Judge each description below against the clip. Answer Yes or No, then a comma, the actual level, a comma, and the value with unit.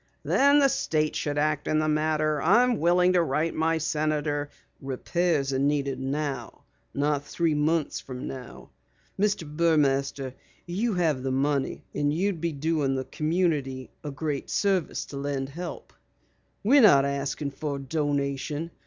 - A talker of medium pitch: Yes, medium, 150 Hz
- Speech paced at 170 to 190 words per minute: No, average, 150 wpm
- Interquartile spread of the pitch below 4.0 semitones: Yes, average, 3.2 semitones